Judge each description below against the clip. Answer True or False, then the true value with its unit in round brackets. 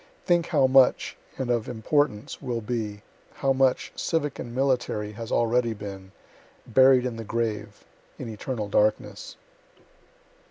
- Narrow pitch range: False (3.6 semitones)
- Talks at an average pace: False (130 wpm)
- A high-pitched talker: False (120 Hz)